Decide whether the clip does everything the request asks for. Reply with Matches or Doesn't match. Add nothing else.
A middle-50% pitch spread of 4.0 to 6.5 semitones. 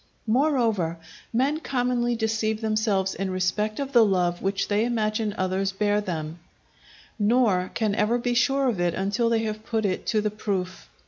Doesn't match